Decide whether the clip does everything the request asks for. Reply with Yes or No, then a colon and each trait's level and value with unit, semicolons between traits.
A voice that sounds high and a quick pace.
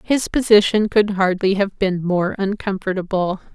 No: high, 195 Hz; slow, 135 wpm